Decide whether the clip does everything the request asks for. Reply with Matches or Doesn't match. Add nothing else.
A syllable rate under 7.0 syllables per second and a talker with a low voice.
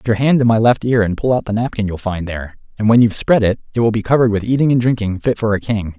Doesn't match